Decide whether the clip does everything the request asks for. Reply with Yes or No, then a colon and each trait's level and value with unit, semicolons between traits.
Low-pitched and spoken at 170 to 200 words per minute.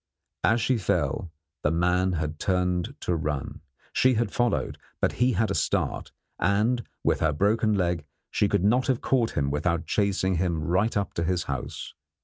Yes: very low, 95 Hz; average, 175 wpm